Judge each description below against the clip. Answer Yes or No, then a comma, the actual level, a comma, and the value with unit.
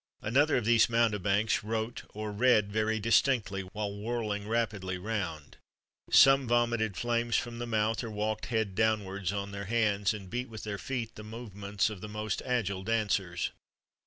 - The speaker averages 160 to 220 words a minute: Yes, average, 165 wpm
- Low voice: Yes, low, 110 Hz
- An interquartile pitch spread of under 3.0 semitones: Yes, narrow, 2.5 semitones